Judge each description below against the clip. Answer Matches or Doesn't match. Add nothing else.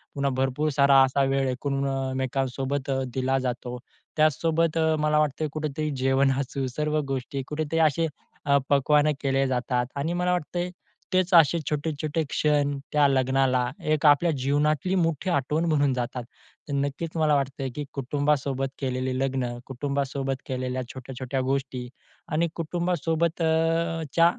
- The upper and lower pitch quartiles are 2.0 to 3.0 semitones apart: Matches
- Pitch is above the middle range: Doesn't match